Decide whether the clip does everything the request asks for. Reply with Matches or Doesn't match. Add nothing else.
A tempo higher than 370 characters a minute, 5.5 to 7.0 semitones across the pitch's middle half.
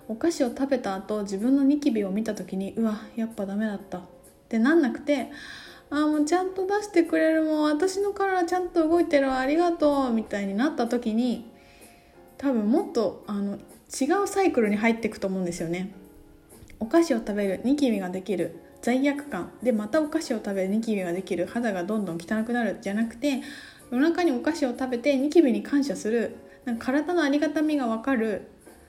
Matches